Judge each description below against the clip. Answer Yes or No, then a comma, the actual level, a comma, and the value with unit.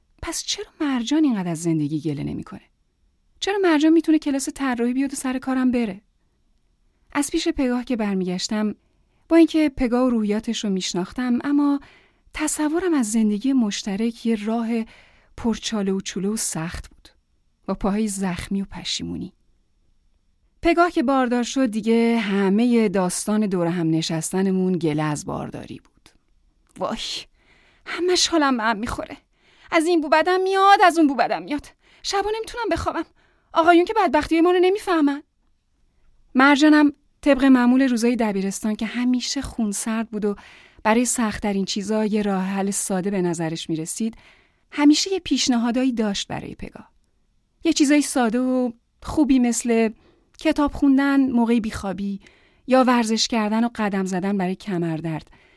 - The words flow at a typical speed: Yes, average, 145 wpm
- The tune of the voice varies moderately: No, wide, 6.2 semitones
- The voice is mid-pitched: No, high, 240 Hz